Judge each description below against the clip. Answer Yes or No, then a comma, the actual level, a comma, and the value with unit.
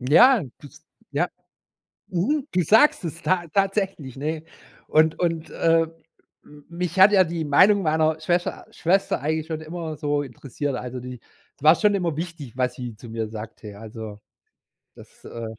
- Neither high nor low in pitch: Yes, medium, 160 Hz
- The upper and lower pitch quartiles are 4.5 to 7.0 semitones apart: Yes, average, 5.2 semitones